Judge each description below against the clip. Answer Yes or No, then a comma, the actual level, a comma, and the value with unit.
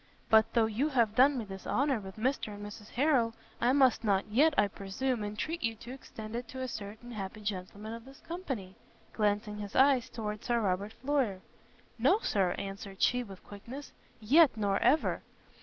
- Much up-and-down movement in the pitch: No, average, 4.1 semitones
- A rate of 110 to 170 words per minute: No, average, 185 wpm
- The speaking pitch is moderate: No, high, 225 Hz